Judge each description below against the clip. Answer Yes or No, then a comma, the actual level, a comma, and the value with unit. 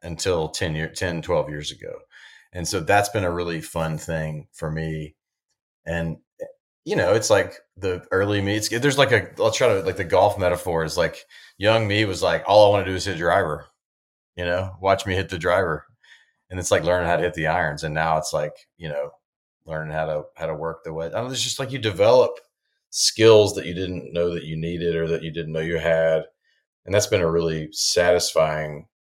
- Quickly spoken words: Yes, fast, 225 wpm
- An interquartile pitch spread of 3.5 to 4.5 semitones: Yes, average, 4.2 semitones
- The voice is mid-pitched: No, very low, 85 Hz